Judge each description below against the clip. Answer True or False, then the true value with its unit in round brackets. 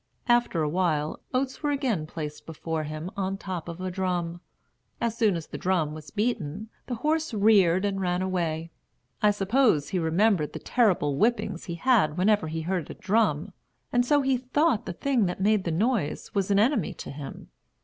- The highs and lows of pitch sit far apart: True (5.7 semitones)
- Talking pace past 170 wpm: True (195 wpm)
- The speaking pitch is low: False (190 Hz)